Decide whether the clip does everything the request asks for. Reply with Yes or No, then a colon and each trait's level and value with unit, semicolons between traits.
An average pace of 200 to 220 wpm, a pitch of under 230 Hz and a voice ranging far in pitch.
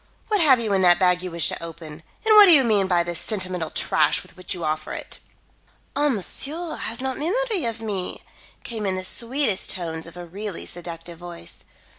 Yes: fast, 205 wpm; high, 190 Hz; wide, 6.8 semitones